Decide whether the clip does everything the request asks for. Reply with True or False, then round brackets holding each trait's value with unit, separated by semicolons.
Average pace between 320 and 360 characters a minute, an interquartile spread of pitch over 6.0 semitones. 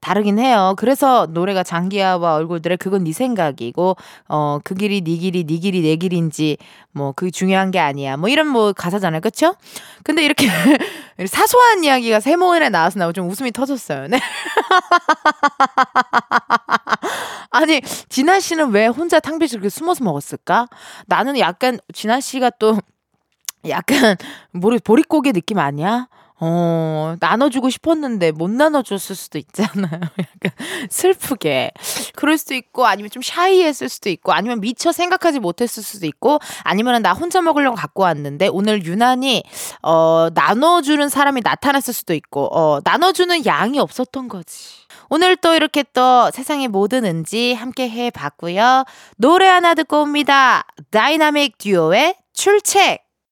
False (310 characters per minute; 8.3 semitones)